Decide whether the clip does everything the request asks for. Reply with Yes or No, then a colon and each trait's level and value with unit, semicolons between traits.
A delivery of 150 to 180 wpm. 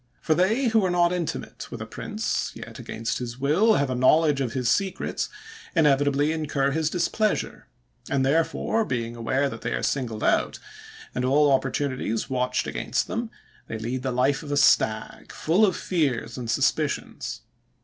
Yes: average, 170 wpm